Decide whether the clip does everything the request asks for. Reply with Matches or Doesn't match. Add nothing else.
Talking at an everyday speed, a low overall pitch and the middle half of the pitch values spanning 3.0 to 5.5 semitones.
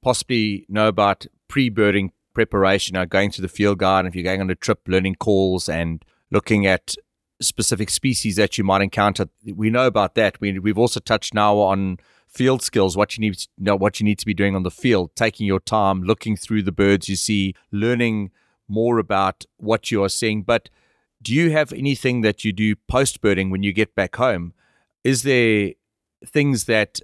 Doesn't match